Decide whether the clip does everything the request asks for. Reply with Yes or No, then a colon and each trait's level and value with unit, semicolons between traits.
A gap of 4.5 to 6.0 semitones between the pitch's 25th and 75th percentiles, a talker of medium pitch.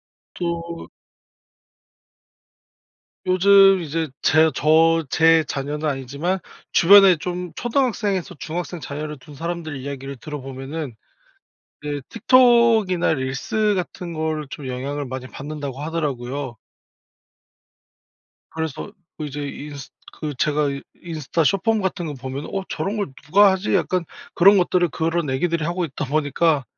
No: average, 4.1 semitones; medium, 160 Hz